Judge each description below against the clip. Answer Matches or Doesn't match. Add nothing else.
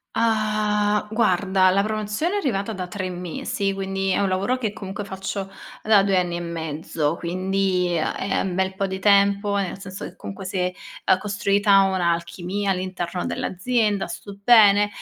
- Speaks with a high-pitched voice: Matches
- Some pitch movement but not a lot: Doesn't match